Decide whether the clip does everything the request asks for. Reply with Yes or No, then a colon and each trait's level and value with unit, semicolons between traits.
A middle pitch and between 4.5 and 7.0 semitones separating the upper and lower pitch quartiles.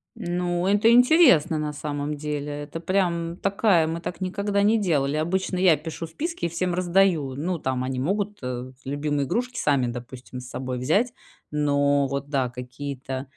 Yes: medium, 155 Hz; average, 5.0 semitones